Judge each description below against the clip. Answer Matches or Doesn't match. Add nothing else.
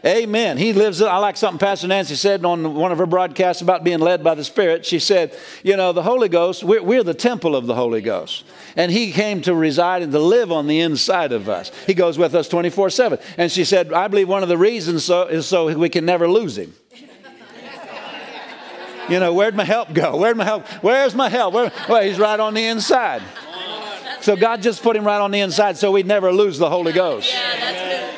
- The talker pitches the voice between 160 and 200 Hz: Matches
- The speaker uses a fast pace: Matches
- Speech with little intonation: Doesn't match